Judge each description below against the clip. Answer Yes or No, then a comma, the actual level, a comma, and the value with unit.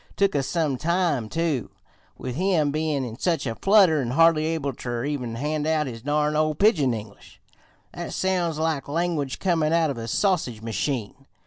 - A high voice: No, medium, 150 Hz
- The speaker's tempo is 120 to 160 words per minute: No, average, 180 wpm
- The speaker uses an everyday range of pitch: Yes, average, 4.3 semitones